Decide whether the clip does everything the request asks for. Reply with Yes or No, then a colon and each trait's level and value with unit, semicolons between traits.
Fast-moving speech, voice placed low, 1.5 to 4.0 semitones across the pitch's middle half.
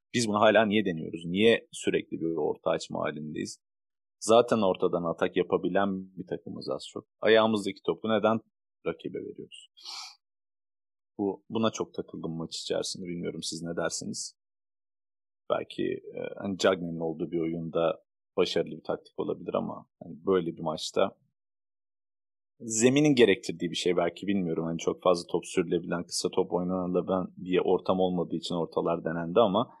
Yes: fast, 145 wpm; very low, 95 Hz; average, 2.9 semitones